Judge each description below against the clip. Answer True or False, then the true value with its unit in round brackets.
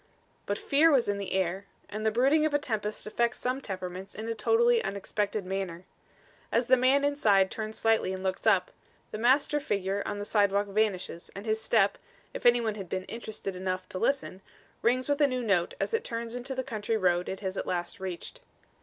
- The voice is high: True (215 Hz)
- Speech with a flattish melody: False (4.4 semitones)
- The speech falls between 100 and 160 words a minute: False (205 wpm)